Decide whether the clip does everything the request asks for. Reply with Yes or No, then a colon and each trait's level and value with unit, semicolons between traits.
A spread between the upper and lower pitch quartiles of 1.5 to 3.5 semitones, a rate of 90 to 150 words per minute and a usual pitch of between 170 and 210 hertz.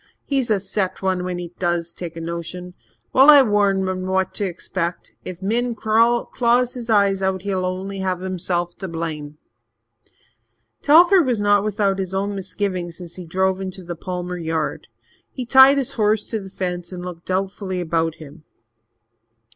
No: average, 2.8 semitones; average, 170 wpm; high, 190 Hz